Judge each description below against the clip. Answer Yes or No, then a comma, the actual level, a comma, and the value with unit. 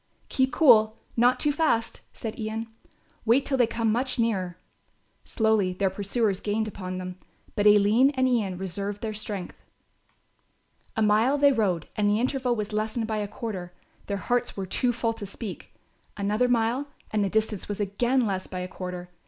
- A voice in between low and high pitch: No, high, 215 Hz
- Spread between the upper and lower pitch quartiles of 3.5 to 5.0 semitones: No, average, 3.1 semitones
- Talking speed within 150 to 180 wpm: Yes, average, 175 wpm